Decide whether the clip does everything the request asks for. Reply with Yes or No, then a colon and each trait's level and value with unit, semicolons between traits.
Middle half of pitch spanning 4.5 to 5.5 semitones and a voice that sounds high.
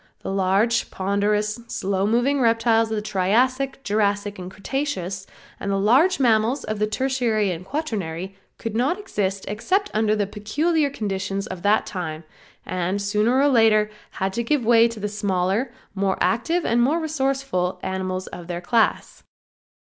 No: average, 4.1 semitones; high, 215 Hz